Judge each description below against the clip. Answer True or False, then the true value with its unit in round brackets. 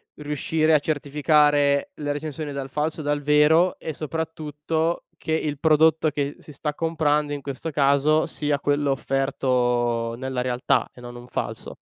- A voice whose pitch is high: False (145 Hz)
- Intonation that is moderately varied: False (2.1 semitones)